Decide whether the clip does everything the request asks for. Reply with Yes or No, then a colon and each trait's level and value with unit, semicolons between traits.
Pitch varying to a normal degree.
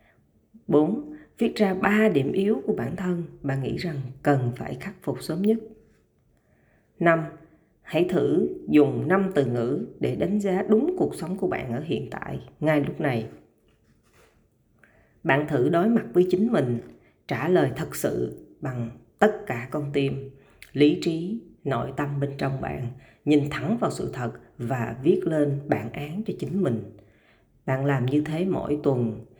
No: wide, 6.1 semitones